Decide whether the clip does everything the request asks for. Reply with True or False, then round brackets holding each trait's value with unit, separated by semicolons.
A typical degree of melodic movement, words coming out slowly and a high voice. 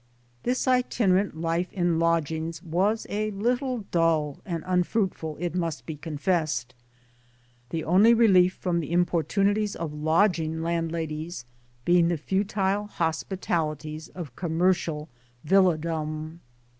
False (3.2 semitones; 115 wpm; 170 Hz)